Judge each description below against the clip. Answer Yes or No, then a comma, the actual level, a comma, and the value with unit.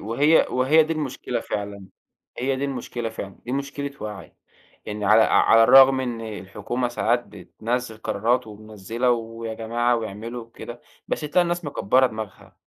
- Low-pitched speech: Yes, low, 120 Hz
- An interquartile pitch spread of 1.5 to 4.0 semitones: Yes, average, 3.2 semitones